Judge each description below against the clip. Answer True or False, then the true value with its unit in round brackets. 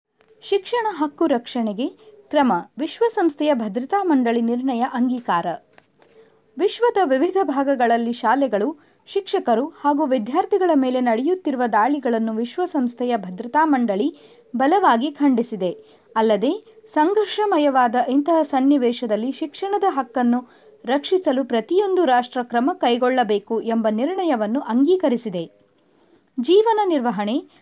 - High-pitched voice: True (275 Hz)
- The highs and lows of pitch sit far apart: True (7.0 semitones)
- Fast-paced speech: False (85 wpm)